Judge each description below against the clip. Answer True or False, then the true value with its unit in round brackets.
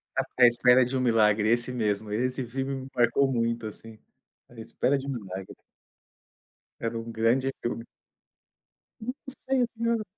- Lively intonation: False (2.8 semitones)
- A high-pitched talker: False (120 Hz)